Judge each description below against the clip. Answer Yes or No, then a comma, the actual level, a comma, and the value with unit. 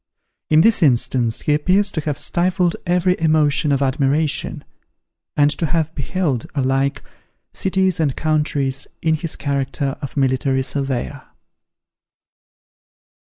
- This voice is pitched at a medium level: Yes, medium, 150 Hz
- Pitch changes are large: No, average, 3.2 semitones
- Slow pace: Yes, slow, 115 wpm